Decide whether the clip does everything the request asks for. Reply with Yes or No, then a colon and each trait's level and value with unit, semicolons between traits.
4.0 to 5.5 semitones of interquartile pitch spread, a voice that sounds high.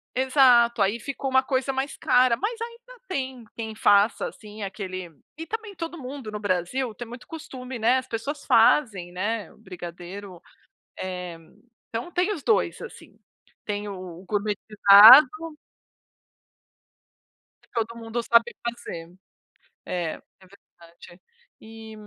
Yes: average, 4.9 semitones; high, 230 Hz